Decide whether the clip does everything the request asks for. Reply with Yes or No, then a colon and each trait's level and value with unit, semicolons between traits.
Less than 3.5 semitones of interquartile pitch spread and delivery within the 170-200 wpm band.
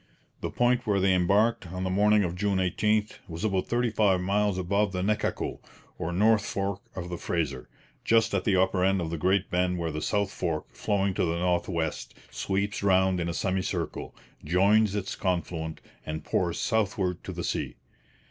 Yes: narrow, 2.6 semitones; average, 185 wpm